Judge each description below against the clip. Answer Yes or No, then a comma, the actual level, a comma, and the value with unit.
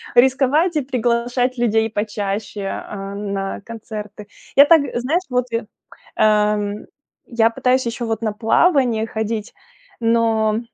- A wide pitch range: No, average, 2.9 semitones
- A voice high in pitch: Yes, high, 225 Hz